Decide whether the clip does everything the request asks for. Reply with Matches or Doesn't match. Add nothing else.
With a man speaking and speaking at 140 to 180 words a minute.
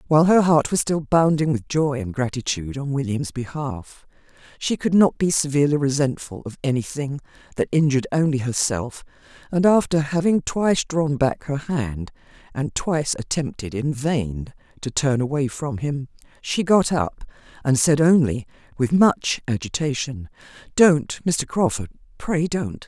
Doesn't match